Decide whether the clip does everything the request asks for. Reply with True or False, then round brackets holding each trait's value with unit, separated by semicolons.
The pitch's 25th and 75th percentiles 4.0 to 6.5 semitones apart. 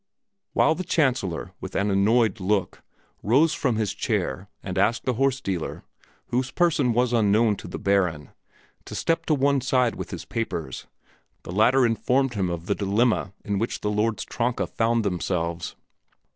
True (4.4 semitones)